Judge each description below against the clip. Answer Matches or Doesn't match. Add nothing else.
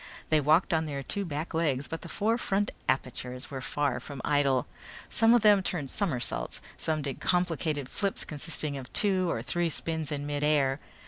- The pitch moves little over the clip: Doesn't match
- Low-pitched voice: Doesn't match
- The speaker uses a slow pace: Doesn't match